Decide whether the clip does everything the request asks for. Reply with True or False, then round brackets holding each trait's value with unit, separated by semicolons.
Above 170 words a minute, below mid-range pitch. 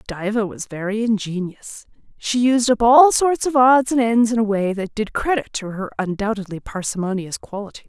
False (185 wpm; 220 Hz)